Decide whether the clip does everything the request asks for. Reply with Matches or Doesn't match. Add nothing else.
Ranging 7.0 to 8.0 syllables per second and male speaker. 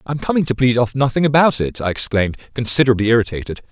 Matches